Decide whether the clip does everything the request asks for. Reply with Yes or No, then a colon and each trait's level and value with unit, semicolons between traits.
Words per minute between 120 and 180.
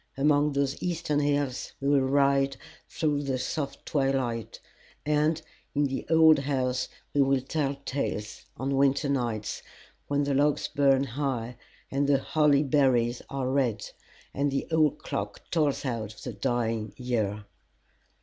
Yes: average, 140 wpm